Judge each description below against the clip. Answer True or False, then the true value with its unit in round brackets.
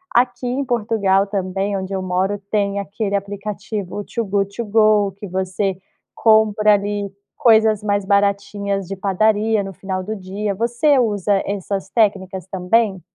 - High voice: True (200 Hz)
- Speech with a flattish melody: True (1.9 semitones)